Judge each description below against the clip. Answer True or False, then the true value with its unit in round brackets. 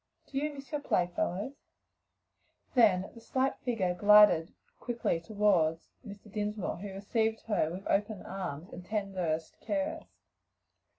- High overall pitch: True (205 Hz)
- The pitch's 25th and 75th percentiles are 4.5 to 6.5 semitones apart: False (3.6 semitones)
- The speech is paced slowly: True (110 wpm)